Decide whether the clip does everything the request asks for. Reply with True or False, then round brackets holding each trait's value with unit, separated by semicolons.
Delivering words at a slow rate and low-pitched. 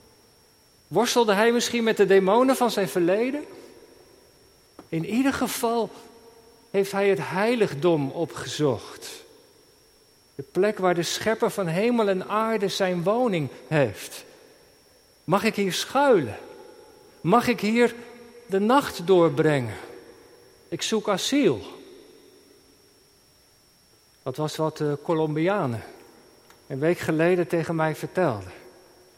False (110 wpm; 220 Hz)